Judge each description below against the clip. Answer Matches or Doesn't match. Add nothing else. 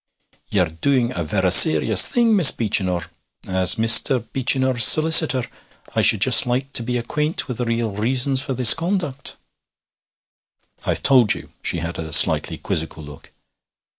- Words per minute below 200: Matches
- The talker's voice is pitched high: Doesn't match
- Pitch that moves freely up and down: Matches